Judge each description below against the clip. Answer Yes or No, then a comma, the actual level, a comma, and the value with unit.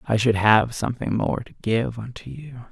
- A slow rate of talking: No, average, 200 wpm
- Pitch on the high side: No, low, 115 Hz